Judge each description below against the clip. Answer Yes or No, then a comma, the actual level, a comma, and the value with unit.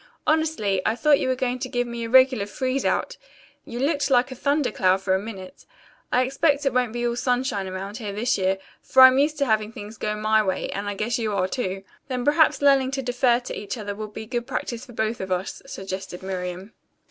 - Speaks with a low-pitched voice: No, high, 235 Hz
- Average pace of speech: No, fast, 230 wpm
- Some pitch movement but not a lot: Yes, average, 4.3 semitones